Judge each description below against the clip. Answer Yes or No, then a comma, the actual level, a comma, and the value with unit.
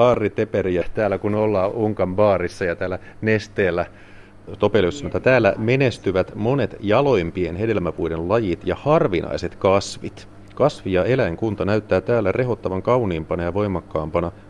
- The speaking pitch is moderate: No, low, 100 Hz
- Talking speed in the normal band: Yes, average, 110 wpm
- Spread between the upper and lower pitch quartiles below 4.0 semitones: Yes, average, 2.8 semitones